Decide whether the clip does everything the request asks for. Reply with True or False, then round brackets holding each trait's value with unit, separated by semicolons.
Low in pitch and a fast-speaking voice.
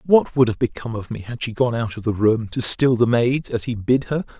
True (120 Hz; 285 wpm)